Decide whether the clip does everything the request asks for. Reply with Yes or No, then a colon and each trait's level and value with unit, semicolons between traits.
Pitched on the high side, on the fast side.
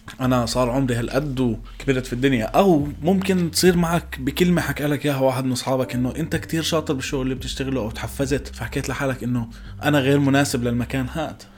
No: low, 135 Hz; fast, 180 wpm